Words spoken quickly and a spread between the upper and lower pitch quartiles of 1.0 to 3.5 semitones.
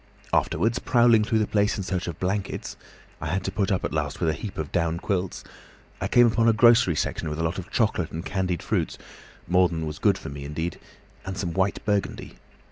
No: fast, 210 wpm; average, 4.2 semitones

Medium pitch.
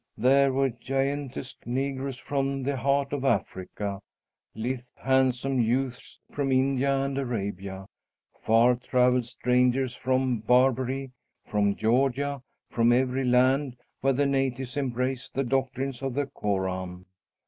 No: low, 130 Hz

